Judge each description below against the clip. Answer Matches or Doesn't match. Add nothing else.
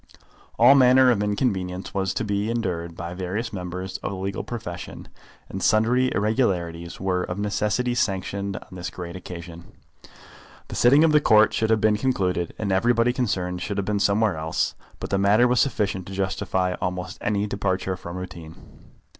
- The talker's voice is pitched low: Matches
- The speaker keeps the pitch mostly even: Doesn't match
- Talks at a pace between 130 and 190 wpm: Matches